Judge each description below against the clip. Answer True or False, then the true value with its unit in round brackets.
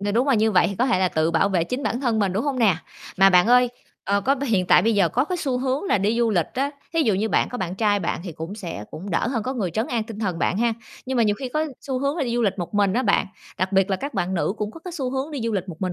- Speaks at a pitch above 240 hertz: False (220 Hz)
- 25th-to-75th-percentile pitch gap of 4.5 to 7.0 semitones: True (5.1 semitones)